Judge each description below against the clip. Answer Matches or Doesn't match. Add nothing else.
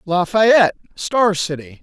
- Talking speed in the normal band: Doesn't match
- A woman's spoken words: Doesn't match